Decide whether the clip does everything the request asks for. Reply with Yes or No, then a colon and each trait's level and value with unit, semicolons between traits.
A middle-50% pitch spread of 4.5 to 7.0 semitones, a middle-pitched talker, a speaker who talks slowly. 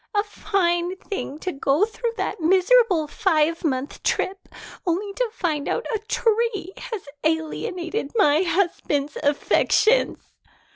No: average, 5.0 semitones; very high, 370 Hz; slow, 125 wpm